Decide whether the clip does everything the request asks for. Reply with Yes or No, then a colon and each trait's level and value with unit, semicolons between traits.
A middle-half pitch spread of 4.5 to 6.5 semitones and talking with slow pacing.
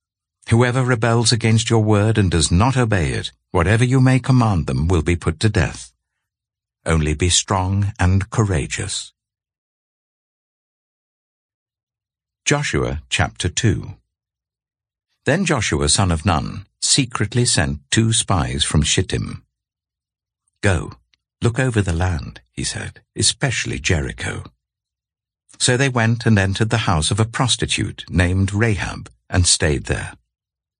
Yes: average, 5.3 semitones; slow, 125 wpm